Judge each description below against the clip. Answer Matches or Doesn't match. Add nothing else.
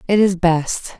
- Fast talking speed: Doesn't match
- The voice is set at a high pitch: Doesn't match